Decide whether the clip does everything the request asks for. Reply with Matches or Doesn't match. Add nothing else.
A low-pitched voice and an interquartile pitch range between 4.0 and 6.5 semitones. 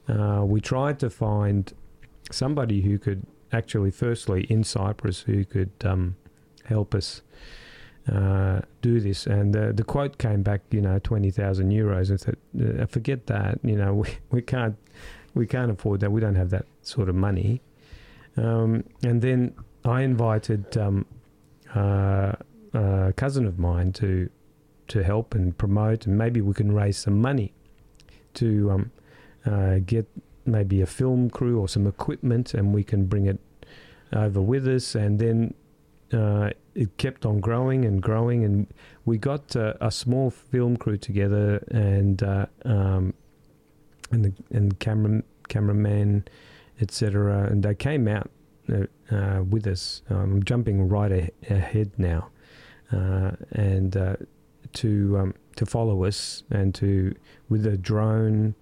Doesn't match